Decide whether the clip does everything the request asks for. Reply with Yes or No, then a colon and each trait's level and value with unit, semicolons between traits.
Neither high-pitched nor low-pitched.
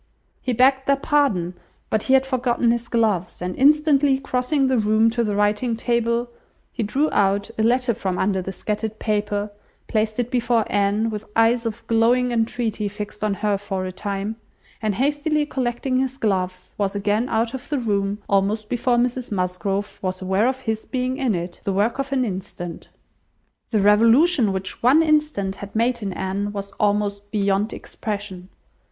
No: high, 220 Hz